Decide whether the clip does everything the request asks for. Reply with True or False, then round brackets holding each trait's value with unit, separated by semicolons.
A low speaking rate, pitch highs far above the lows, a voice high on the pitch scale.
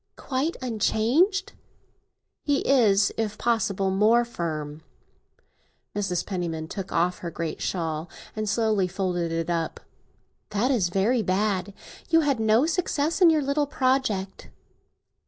True (125 wpm; 6.2 semitones; 210 Hz)